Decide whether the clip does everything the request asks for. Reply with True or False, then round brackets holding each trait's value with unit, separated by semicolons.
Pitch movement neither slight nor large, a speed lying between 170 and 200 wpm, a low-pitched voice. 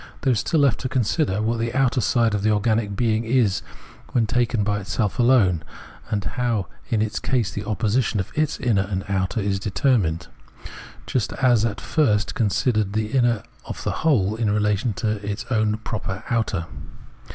True (3.0 semitones; 185 wpm; 110 Hz)